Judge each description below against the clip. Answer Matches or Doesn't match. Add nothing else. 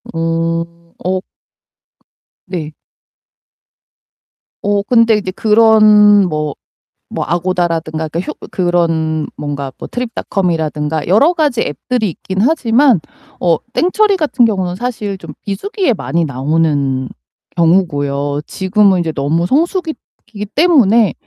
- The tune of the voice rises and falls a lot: Matches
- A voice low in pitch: Doesn't match